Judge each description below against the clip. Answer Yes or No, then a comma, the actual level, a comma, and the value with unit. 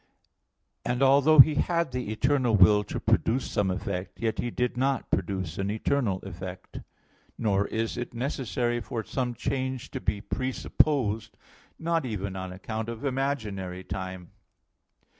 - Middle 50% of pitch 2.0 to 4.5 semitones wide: No, average, 5.1 semitones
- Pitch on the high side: No, low, 115 Hz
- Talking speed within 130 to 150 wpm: Yes, average, 140 wpm